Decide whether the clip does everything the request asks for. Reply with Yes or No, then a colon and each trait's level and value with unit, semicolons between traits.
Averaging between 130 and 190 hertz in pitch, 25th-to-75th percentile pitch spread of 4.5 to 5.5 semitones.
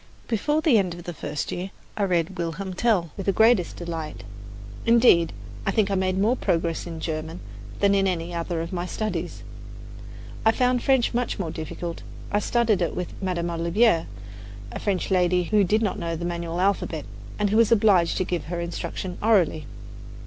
No: medium, 185 Hz; average, 3.8 semitones